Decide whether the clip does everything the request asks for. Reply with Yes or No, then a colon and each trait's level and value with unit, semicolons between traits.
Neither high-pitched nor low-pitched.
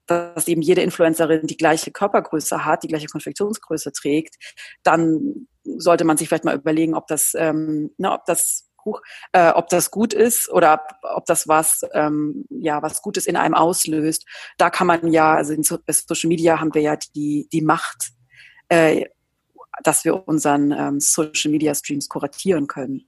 Yes: medium, 160 Hz